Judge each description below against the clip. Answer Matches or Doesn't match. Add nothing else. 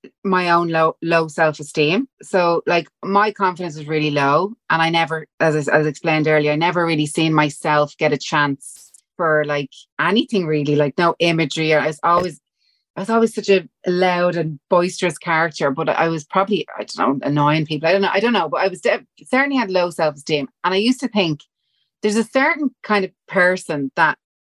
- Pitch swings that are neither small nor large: Matches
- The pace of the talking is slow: Doesn't match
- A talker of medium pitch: Matches